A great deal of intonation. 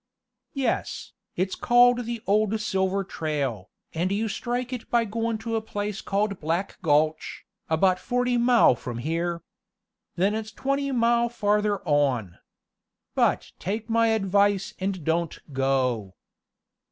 Yes: wide, 5.9 semitones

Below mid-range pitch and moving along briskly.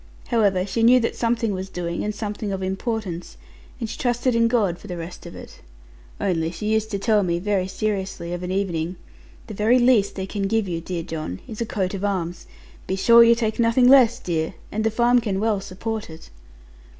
No: high, 205 Hz; fast, 210 wpm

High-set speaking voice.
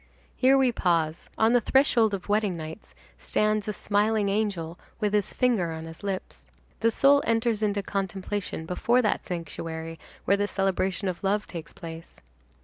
Yes: high, 200 Hz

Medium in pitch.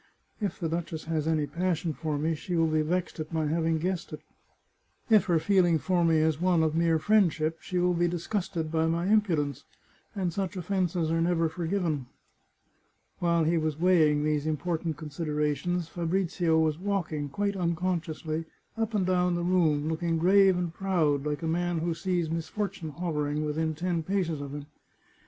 Yes: medium, 165 Hz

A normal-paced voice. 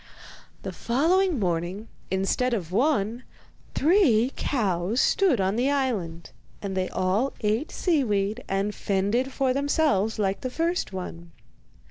No: slow, 125 wpm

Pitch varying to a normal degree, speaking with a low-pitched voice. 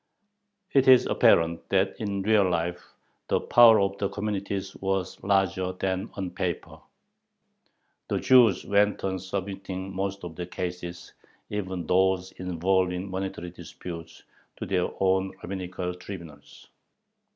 No: narrow, 1.7 semitones; very low, 95 Hz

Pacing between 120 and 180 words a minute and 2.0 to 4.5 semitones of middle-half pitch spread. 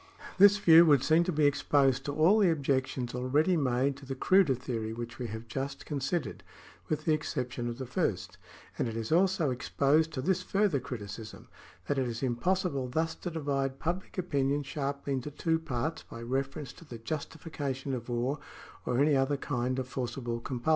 No: average, 190 wpm; average, 4.0 semitones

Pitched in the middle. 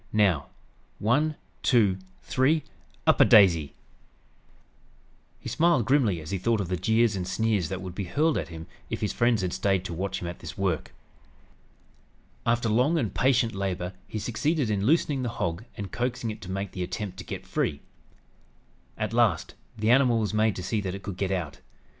No: low, 105 Hz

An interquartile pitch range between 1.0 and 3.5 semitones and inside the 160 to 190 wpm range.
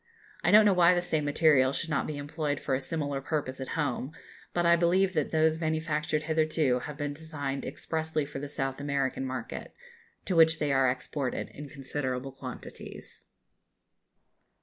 Yes: average, 2.7 semitones; average, 170 wpm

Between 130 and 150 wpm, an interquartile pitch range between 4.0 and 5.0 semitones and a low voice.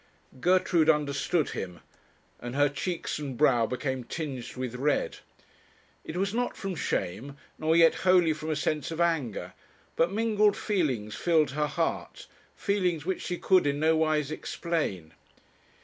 No: average, 145 wpm; average, 4.3 semitones; medium, 155 Hz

